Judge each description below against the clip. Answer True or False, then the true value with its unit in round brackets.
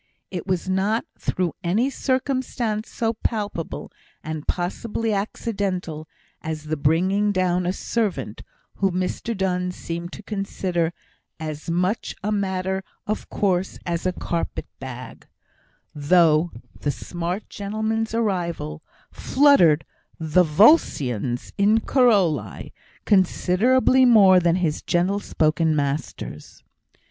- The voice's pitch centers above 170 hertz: True (185 Hz)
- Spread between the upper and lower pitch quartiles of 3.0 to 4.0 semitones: False (4.4 semitones)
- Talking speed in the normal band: False (110 wpm)